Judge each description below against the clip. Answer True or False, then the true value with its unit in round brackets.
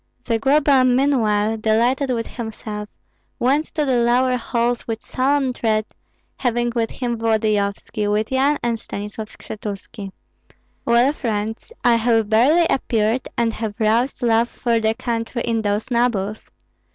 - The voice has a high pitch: True (230 Hz)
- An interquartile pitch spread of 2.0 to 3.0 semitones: True (2.5 semitones)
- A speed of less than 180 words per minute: True (135 wpm)